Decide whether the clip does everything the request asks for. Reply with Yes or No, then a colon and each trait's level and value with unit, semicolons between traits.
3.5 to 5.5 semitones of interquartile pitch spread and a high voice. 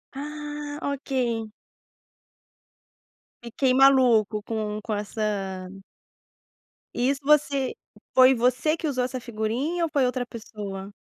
Yes: average, 4.4 semitones; very high, 250 Hz